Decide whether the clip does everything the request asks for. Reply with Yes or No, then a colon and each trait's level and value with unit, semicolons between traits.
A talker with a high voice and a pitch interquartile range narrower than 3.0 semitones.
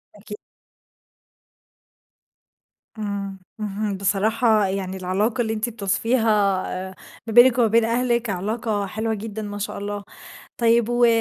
Yes: high, 215 Hz; narrow, 2.4 semitones